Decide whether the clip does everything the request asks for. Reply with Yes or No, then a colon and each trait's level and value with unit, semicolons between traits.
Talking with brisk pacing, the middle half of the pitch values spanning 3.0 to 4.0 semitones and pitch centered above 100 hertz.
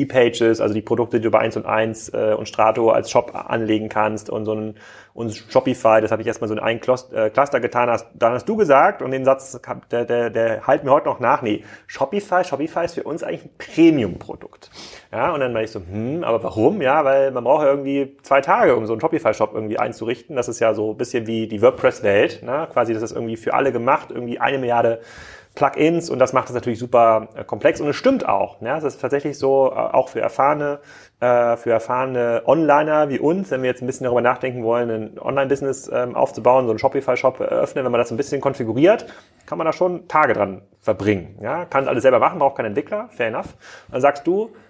Yes: fast, 225 wpm; average, 3.5 semitones; low, 120 Hz